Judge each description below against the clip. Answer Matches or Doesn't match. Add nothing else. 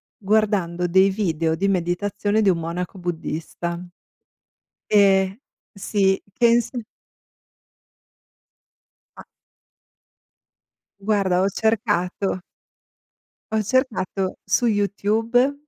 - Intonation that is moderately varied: Matches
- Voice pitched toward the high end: Matches